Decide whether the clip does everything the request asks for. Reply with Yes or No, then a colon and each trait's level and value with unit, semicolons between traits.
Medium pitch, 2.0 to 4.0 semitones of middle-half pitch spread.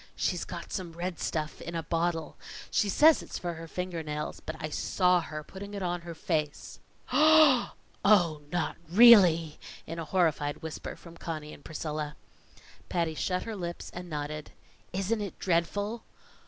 Yes: medium, 170 Hz; average, 3.2 semitones